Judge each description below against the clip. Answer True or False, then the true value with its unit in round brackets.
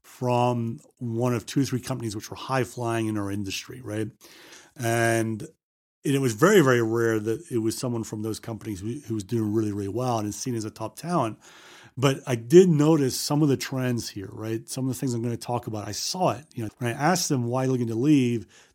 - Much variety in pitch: False (2.9 semitones)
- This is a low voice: True (120 Hz)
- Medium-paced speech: False (235 wpm)